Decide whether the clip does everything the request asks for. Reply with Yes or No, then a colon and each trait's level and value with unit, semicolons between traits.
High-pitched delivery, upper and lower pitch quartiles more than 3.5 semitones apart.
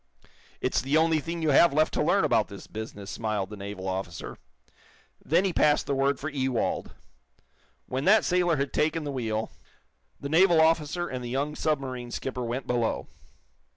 No: medium, 140 Hz; average, 5.1 semitones